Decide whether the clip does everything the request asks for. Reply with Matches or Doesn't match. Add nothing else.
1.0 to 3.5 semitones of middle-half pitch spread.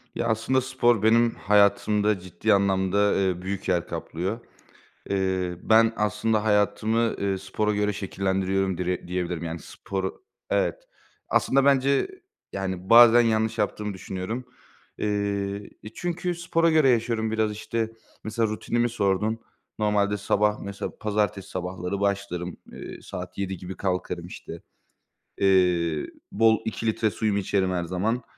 Matches